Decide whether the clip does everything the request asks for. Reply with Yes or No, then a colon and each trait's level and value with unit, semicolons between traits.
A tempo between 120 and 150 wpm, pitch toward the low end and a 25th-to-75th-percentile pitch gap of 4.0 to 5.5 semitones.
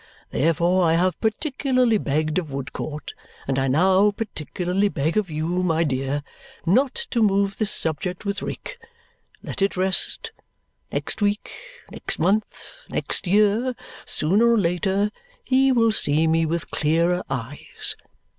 No: slow, 135 wpm; medium, 185 Hz; average, 5.0 semitones